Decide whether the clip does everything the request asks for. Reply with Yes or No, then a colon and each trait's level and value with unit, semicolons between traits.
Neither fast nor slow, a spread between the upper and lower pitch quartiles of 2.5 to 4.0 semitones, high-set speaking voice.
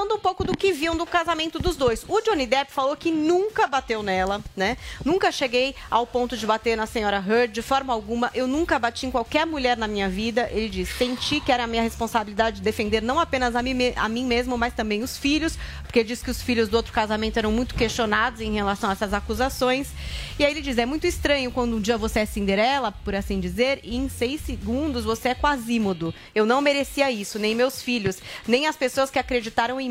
No: fast, 220 wpm; average, 3.5 semitones; high, 245 Hz